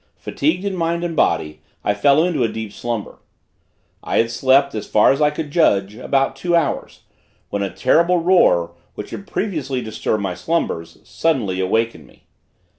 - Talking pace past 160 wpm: Yes, average, 170 wpm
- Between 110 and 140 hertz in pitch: Yes, low, 135 Hz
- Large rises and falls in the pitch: Yes, wide, 7.7 semitones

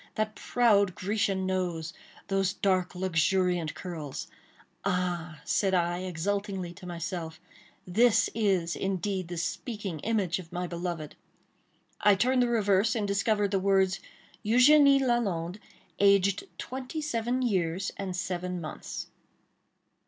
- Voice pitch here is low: No, high, 190 Hz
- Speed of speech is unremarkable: No, slow, 110 wpm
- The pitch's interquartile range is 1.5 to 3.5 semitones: Yes, average, 3.0 semitones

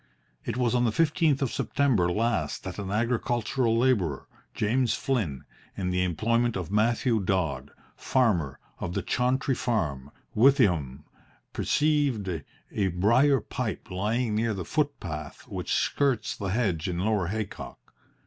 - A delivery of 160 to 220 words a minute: No, slow, 135 wpm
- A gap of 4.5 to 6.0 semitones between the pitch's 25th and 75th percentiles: Yes, wide, 5.4 semitones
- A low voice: Yes, low, 110 Hz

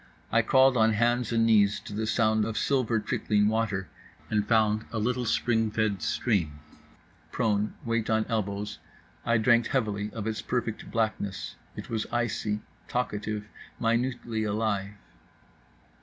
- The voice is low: Yes, low, 110 Hz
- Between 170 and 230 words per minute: No, average, 140 wpm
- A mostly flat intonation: Yes, narrow, 1.9 semitones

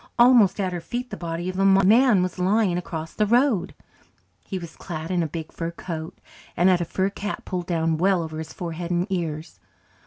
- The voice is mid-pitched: Yes, medium, 180 Hz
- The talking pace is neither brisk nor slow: No, fast, 210 wpm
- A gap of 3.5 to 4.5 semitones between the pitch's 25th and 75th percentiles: No, average, 2.8 semitones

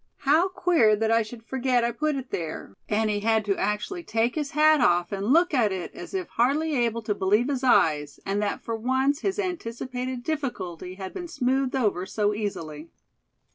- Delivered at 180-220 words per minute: Yes, average, 195 wpm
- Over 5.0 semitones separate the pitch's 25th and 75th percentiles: Yes, wide, 5.5 semitones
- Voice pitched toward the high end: Yes, high, 235 Hz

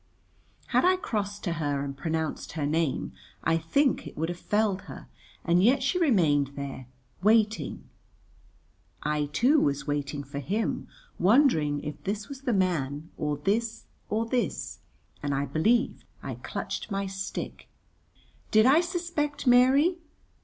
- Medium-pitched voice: No, high, 195 Hz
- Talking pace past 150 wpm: No, average, 145 wpm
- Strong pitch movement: Yes, wide, 8.7 semitones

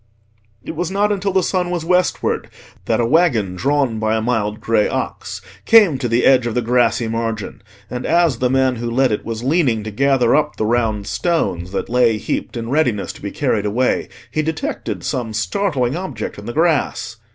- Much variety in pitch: Yes, wide, 6.0 semitones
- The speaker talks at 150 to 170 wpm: No, average, 195 wpm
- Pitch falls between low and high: No, low, 125 Hz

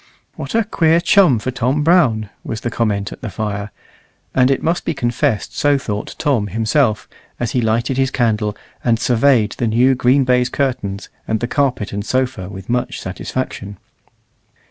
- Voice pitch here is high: No, low, 120 Hz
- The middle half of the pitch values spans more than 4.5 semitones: No, average, 3.9 semitones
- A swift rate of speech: No, average, 170 wpm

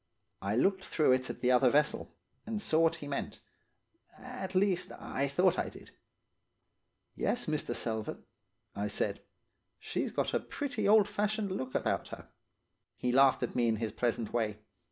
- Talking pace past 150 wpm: Yes, average, 165 wpm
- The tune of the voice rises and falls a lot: Yes, wide, 8.6 semitones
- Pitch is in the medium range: Yes, medium, 145 Hz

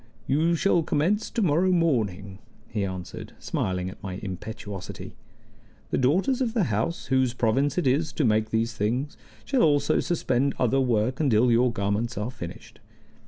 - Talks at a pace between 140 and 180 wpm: Yes, average, 160 wpm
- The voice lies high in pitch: No, low, 125 Hz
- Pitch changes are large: Yes, wide, 6.5 semitones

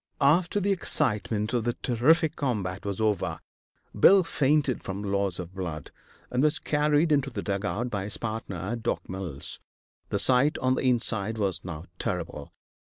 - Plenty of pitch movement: Yes, wide, 5.7 semitones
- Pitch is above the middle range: No, low, 110 Hz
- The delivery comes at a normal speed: Yes, average, 160 wpm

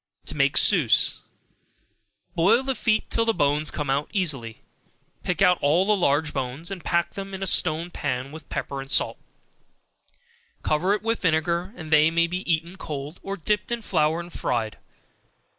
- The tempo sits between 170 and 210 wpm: Yes, average, 175 wpm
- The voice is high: No, medium, 170 Hz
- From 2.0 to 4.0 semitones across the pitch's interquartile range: No, average, 4.6 semitones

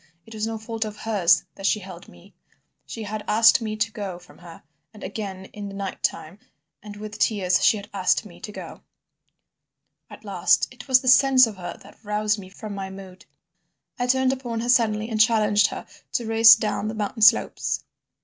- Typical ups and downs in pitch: No, narrow, 2.2 semitones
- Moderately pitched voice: No, high, 215 Hz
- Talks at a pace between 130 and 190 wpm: No, average, 200 wpm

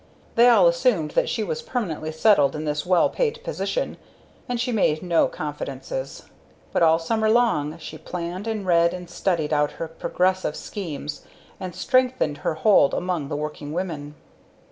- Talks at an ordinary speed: Yes, average, 165 wpm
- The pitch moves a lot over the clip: Yes, wide, 6.2 semitones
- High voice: No, medium, 170 Hz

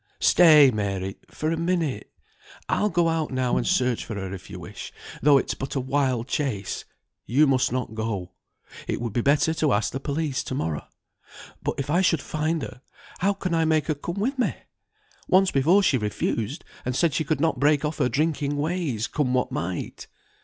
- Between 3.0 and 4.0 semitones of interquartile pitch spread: No, average, 4.6 semitones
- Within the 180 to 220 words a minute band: Yes, average, 195 wpm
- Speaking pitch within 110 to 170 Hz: Yes, medium, 140 Hz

